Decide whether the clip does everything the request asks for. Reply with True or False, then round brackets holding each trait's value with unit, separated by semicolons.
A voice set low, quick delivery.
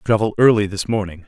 False (105 Hz; 190 wpm)